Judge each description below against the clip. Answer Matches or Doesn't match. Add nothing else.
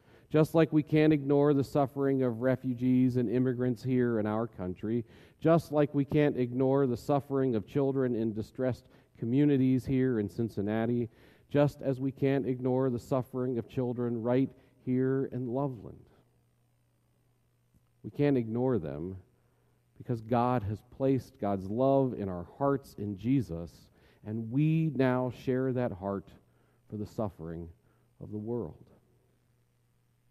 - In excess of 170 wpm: Doesn't match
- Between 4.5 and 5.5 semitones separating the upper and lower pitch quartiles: Doesn't match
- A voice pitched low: Matches